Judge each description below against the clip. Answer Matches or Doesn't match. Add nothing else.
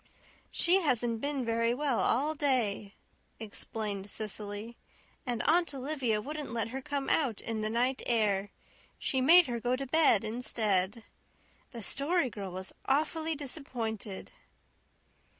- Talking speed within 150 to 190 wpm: Doesn't match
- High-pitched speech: Matches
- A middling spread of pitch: Matches